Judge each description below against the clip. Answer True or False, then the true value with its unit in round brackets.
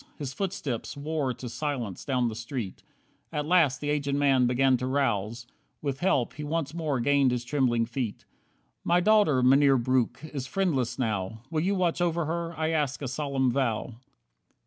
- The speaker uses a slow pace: False (170 wpm)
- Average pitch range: True (3.8 semitones)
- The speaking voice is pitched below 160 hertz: True (135 Hz)